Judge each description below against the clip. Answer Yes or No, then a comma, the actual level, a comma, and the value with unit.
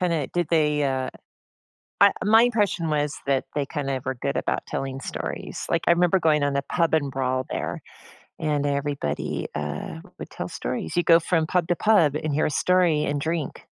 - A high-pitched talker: No, medium, 150 Hz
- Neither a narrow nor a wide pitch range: Yes, average, 3.5 semitones